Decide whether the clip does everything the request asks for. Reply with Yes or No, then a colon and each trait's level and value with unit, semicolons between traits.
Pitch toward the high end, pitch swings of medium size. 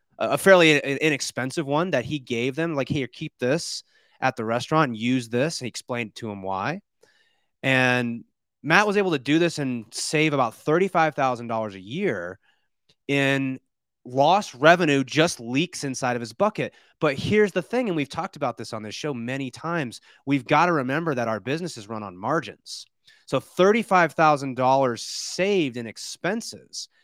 No: medium, 140 Hz; average, 5.0 semitones